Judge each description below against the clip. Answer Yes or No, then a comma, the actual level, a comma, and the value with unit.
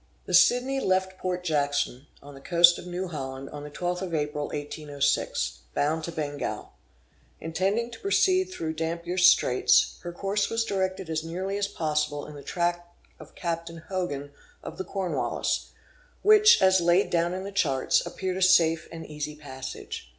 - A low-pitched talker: No, medium, 170 Hz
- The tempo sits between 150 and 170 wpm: Yes, average, 165 wpm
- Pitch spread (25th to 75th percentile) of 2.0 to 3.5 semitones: No, average, 4.1 semitones